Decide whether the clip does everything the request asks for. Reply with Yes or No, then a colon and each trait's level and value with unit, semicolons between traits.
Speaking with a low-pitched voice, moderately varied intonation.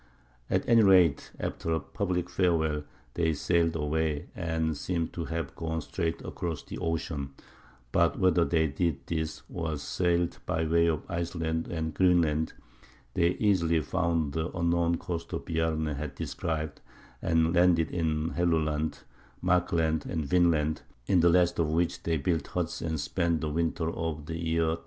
No: very low, 80 Hz; narrow, 1.5 semitones